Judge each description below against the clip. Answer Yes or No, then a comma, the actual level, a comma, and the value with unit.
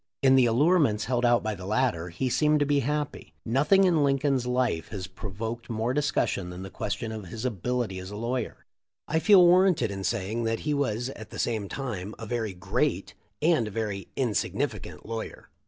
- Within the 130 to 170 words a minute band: No, average, 195 wpm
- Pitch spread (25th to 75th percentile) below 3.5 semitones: No, average, 4.6 semitones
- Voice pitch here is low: Yes, low, 120 Hz